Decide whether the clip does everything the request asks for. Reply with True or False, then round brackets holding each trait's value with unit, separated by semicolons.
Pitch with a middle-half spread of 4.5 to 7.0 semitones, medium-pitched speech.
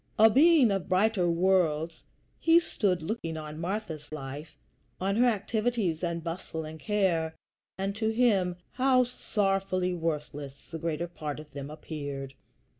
True (5.2 semitones; 180 Hz)